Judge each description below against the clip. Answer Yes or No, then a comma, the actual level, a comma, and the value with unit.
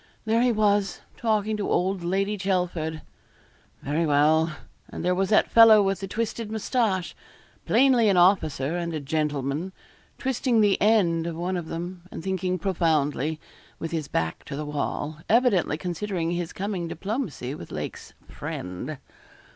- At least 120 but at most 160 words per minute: Yes, average, 150 wpm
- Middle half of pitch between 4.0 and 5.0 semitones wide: Yes, average, 4.6 semitones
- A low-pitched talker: No, medium, 180 Hz